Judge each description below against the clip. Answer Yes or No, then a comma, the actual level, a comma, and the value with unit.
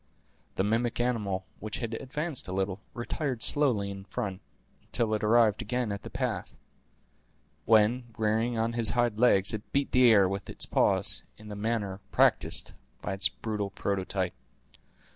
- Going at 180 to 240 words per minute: No, average, 160 wpm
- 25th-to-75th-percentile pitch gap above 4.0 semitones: No, average, 3.1 semitones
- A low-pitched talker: Yes, low, 110 Hz